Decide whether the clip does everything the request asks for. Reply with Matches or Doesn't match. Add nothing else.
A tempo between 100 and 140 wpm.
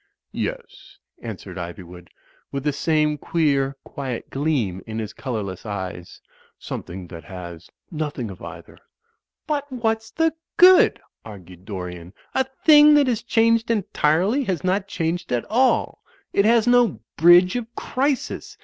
Matches